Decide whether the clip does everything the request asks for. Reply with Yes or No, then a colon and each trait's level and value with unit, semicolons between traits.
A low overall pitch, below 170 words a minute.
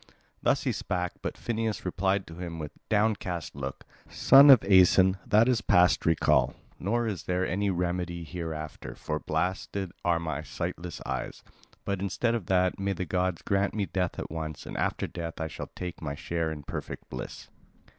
No: very low, 90 Hz; average, 175 wpm